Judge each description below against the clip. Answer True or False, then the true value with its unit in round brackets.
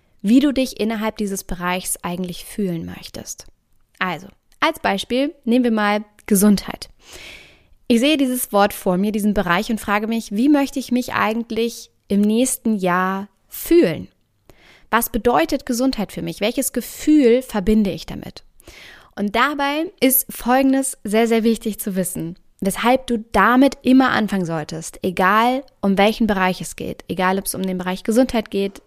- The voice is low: False (220 Hz)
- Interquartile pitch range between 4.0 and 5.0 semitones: True (4.3 semitones)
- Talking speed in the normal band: True (155 wpm)